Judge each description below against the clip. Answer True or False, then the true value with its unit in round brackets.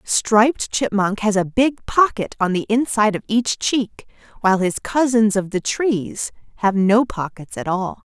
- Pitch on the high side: True (215 Hz)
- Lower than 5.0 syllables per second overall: True (4.3 syllables/s)